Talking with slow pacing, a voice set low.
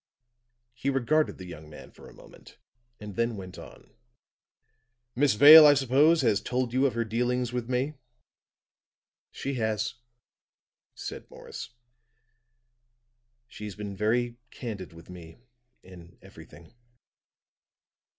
Yes: slow, 120 wpm; low, 115 Hz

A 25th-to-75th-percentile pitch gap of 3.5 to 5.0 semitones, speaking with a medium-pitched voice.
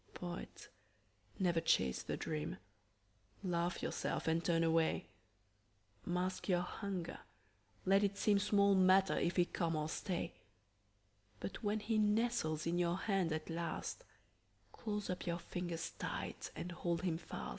No: average, 2.9 semitones; medium, 175 Hz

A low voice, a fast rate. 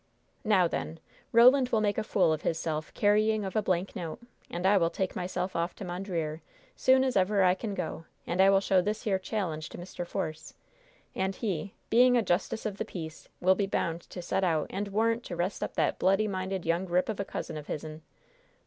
No: high, 190 Hz; fast, 215 wpm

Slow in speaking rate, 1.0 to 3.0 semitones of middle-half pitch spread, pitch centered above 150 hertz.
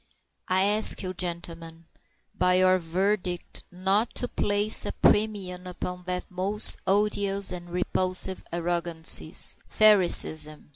Yes: slow, 115 wpm; narrow, 2.4 semitones; medium, 185 Hz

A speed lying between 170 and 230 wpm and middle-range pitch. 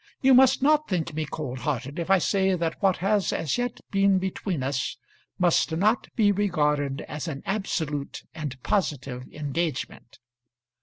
No: average, 155 wpm; medium, 165 Hz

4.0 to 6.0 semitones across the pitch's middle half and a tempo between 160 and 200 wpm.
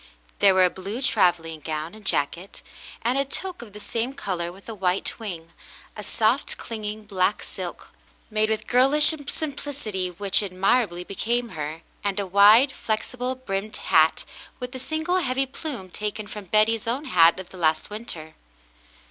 Yes: average, 5.3 semitones; average, 165 wpm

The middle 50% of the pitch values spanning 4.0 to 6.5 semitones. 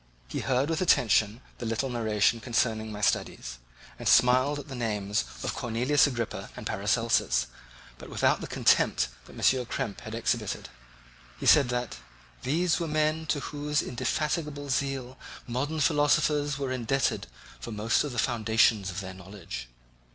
Yes: average, 4.8 semitones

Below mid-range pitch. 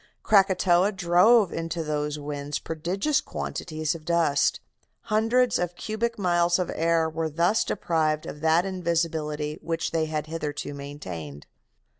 No: medium, 165 Hz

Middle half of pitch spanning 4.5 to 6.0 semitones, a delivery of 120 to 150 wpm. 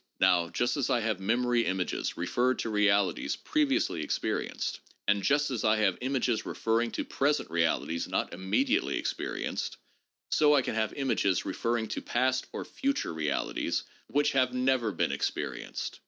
No: wide, 5.4 semitones; average, 165 wpm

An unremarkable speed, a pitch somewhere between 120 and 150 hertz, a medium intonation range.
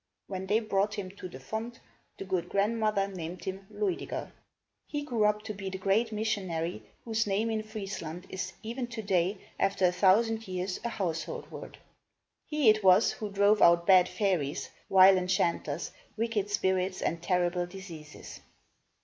No: average, 165 wpm; high, 195 Hz; average, 3.0 semitones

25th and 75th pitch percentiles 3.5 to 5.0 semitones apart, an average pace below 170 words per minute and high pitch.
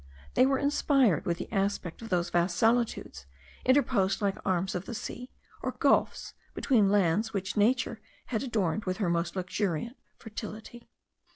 Yes: average, 4.4 semitones; average, 155 wpm; high, 205 Hz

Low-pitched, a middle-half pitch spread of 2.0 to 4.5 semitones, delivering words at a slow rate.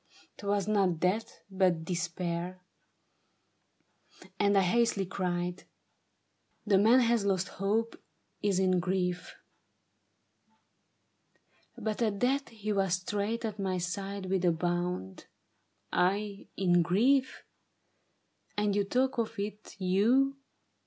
No: high, 195 Hz; average, 2.9 semitones; slow, 120 wpm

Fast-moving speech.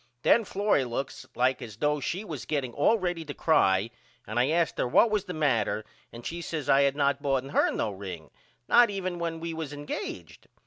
Yes: fast, 210 wpm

